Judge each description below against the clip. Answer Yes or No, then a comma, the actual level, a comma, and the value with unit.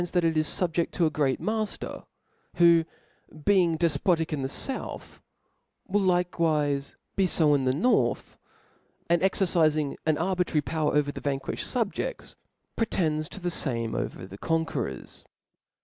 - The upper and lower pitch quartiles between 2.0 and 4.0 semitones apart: Yes, average, 3.4 semitones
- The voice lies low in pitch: No, medium, 165 Hz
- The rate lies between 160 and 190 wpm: No, average, 145 wpm